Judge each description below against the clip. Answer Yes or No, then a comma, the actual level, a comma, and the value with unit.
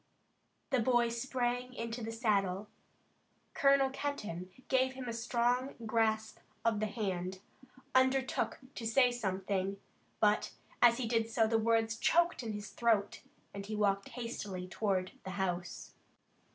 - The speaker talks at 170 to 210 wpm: No, average, 140 wpm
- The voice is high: Yes, high, 225 Hz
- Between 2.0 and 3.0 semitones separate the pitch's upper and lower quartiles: No, average, 3.5 semitones